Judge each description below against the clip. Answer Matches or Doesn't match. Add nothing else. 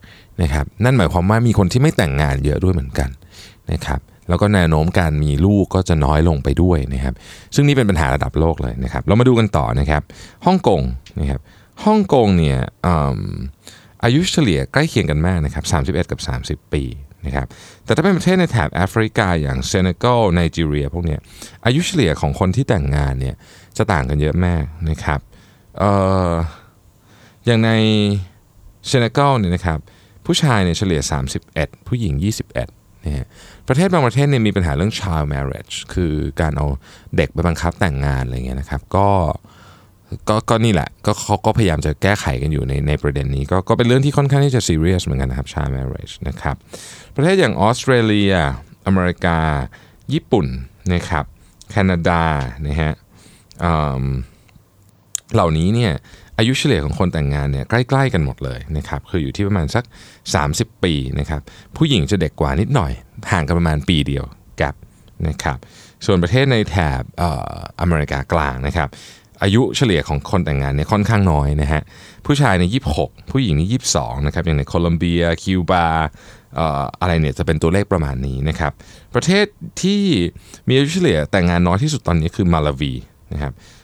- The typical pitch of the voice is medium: Doesn't match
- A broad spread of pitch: Matches